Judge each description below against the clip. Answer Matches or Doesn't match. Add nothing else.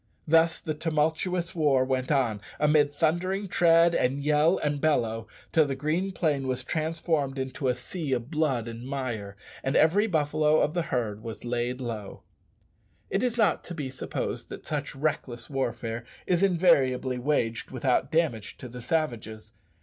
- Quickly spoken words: Doesn't match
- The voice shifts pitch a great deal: Doesn't match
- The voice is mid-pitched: Matches